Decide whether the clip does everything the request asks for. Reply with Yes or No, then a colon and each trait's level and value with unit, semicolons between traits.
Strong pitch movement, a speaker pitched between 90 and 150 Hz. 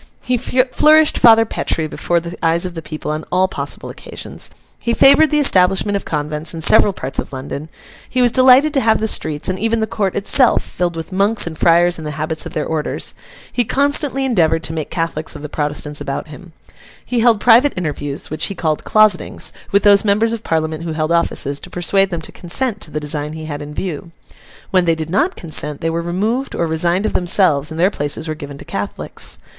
No: wide, 5.8 semitones; medium, 175 Hz